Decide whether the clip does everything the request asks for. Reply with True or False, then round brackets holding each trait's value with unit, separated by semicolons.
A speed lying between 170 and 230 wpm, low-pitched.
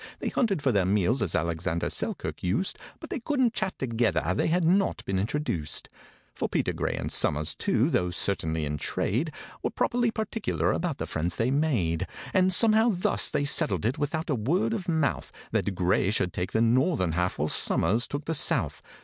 True (185 wpm; 125 Hz)